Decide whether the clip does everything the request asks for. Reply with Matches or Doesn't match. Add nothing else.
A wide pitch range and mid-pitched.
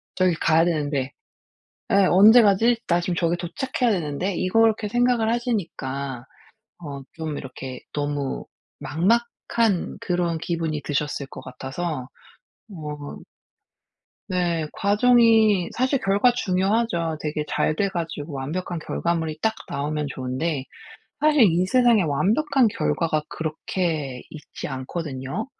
Matches